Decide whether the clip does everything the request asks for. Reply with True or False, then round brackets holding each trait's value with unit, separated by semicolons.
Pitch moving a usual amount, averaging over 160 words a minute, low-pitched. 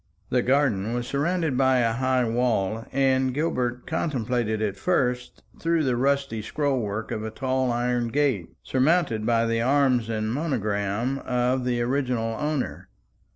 False (3.2 semitones; 150 wpm; 125 Hz)